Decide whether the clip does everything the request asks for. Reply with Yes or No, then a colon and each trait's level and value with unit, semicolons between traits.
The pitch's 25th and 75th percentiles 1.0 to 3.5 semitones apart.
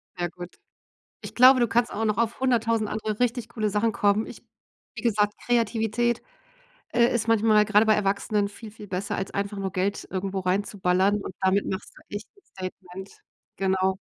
Yes: average, 2.8 semitones